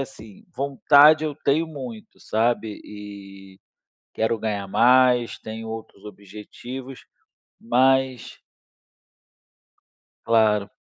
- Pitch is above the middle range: No, low, 115 Hz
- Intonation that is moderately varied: Yes, average, 4.0 semitones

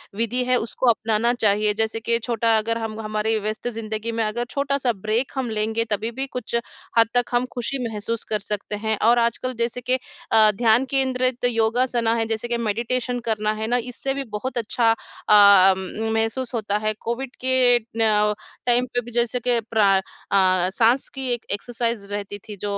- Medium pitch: No, high, 230 Hz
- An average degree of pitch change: No, narrow, 2.2 semitones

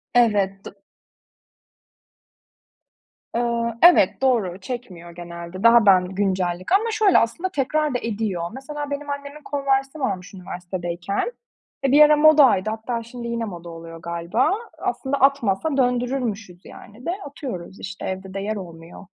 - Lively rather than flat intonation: Yes, wide, 6.6 semitones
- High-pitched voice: Yes, high, 225 Hz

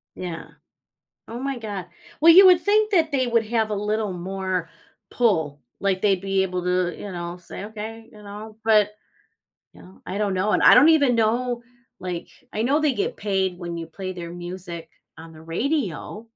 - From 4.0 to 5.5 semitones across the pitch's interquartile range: Yes, average, 4.7 semitones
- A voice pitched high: Yes, high, 205 Hz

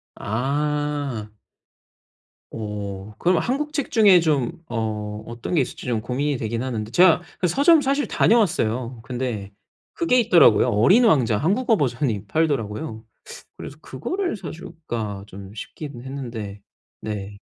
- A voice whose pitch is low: Yes, low, 130 Hz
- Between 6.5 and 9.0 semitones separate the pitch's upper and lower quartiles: Yes, wide, 8.0 semitones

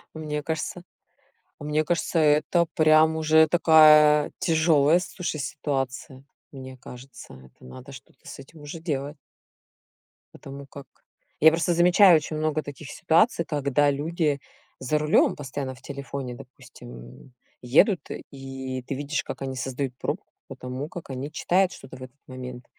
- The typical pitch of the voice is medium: Yes, medium, 145 Hz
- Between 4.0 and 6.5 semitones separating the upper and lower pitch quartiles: No, average, 3.1 semitones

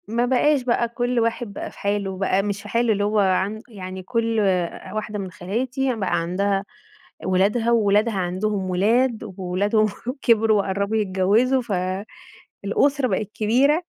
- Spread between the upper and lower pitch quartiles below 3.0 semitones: No, average, 3.4 semitones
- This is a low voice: No, high, 210 Hz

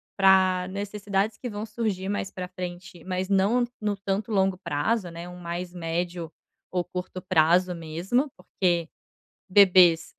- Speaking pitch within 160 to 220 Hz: Yes, medium, 185 Hz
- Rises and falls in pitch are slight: Yes, narrow, 2.3 semitones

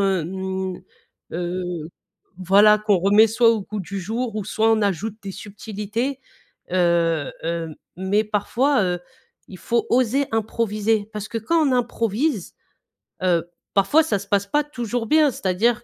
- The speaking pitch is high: Yes, high, 210 Hz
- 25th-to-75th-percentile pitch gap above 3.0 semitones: Yes, average, 3.5 semitones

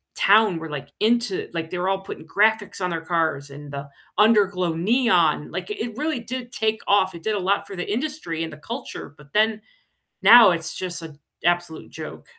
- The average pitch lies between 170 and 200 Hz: Yes, medium, 185 Hz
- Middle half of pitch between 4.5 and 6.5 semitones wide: Yes, average, 5.0 semitones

